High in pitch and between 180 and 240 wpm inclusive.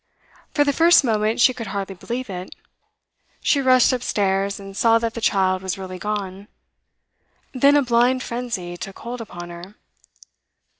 No: high, 215 Hz; average, 155 wpm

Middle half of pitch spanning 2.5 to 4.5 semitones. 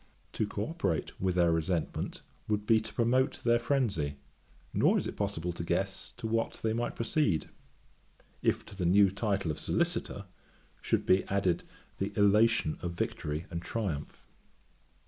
No: average, 4.9 semitones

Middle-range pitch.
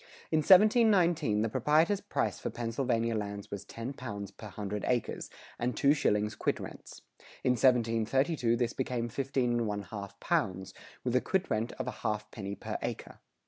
No: low, 115 Hz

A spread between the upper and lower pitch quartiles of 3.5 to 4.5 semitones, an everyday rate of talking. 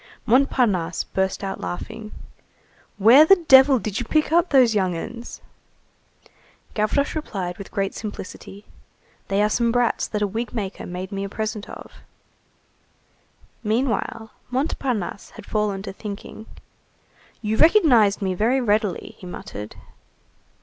No: average, 4.1 semitones; slow, 130 wpm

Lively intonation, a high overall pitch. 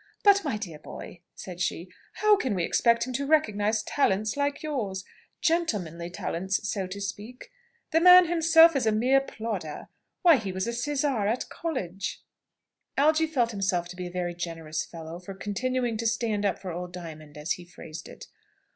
Yes: wide, 7.2 semitones; high, 210 Hz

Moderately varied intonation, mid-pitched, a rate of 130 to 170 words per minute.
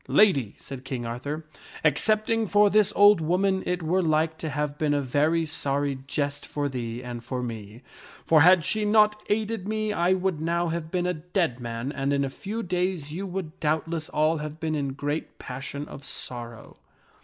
No: average, 4.9 semitones; medium, 155 Hz; average, 195 wpm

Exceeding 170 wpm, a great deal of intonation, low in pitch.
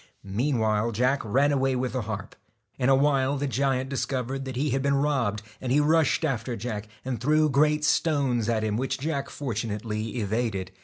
No: average, 190 wpm; average, 3.8 semitones; low, 130 Hz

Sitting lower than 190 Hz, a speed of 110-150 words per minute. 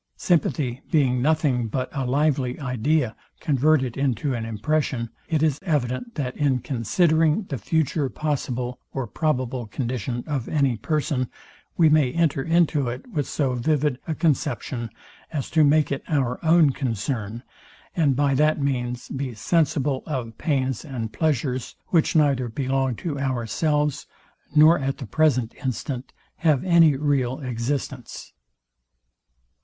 Yes: low, 135 Hz; slow, 135 wpm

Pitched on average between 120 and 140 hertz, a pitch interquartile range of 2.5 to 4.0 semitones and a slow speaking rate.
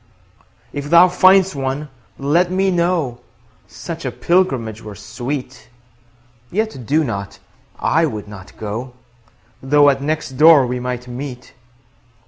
No: low, 135 Hz; average, 5.3 semitones; slow, 130 wpm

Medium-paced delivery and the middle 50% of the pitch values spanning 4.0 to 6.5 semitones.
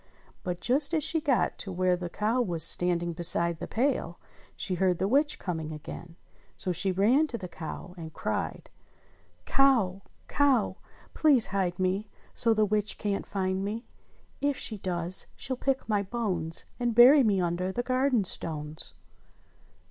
Yes: average, 160 wpm; wide, 5.6 semitones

